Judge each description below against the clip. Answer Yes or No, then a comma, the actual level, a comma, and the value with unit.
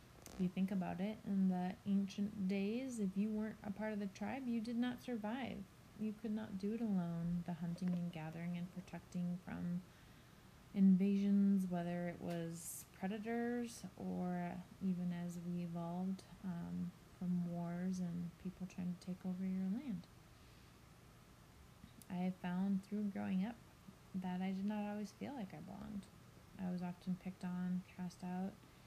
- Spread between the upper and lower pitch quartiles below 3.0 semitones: Yes, narrow, 2.4 semitones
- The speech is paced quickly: No, average, 160 wpm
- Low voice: No, medium, 185 Hz